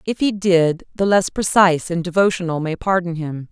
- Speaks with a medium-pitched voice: Yes, medium, 180 Hz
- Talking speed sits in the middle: Yes, average, 190 wpm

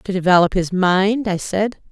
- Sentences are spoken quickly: No, average, 190 wpm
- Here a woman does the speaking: Yes, female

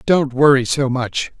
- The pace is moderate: Yes, average, 170 wpm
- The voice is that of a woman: No, male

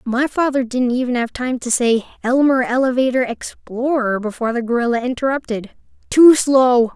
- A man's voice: No, female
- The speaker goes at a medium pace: Yes, average, 145 wpm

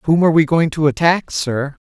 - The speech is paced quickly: Yes, fast, 225 wpm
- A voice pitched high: No, medium, 155 Hz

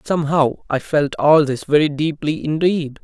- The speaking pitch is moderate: Yes, medium, 150 Hz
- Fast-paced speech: No, average, 160 wpm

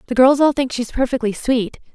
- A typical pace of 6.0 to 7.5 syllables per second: Yes, 6.1 syllables/s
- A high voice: Yes, very high, 250 Hz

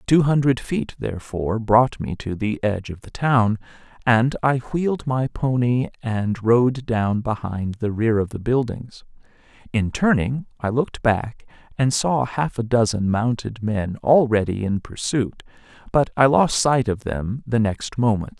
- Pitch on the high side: No, low, 120 Hz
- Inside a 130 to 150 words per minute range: No, average, 165 wpm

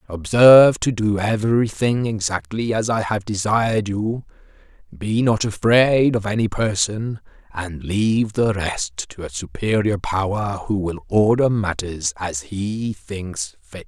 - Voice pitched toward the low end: Yes, low, 105 Hz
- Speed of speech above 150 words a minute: No, average, 140 wpm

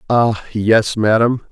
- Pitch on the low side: Yes, low, 110 Hz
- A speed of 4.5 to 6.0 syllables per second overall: No, 3.3 syllables/s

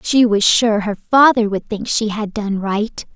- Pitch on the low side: No, high, 215 Hz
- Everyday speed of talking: No, fast, 210 wpm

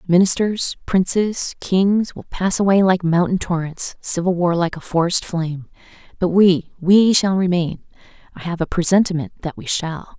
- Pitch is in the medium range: Yes, medium, 180 Hz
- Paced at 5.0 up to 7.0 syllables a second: No, 4.6 syllables/s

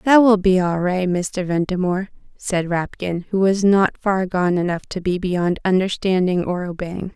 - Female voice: Yes, female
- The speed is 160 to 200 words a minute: Yes, average, 175 wpm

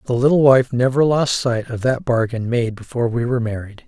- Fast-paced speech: Yes, fast, 215 wpm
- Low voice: Yes, low, 125 Hz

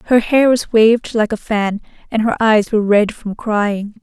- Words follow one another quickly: Yes, fast, 210 wpm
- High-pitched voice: Yes, high, 220 Hz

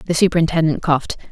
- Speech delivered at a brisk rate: No, slow, 135 wpm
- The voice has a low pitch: No, medium, 160 Hz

